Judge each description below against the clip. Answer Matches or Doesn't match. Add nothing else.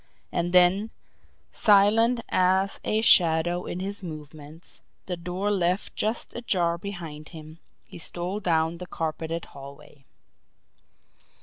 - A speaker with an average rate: Doesn't match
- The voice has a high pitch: Doesn't match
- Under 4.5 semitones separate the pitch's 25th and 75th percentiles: Matches